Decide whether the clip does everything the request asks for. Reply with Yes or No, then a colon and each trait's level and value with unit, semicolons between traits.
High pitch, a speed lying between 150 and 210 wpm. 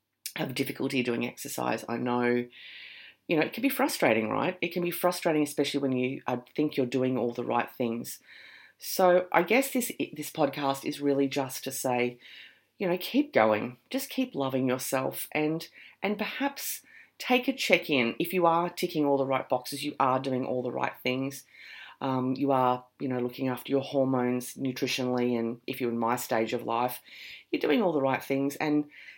No: low, 135 Hz; average, 195 wpm